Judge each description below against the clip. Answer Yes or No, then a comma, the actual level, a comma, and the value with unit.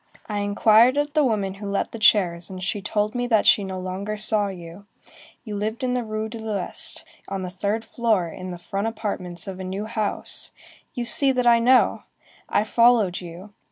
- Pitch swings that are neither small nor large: Yes, average, 3.2 semitones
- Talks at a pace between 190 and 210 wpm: Yes, average, 195 wpm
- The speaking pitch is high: Yes, high, 210 Hz